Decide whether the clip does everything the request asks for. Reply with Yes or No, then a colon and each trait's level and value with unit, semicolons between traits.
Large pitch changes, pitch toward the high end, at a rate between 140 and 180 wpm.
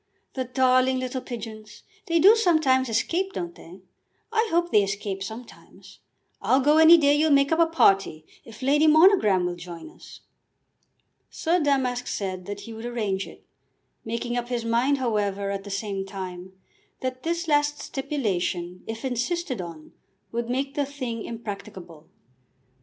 Yes: wide, 6.4 semitones; high, 240 Hz; average, 155 wpm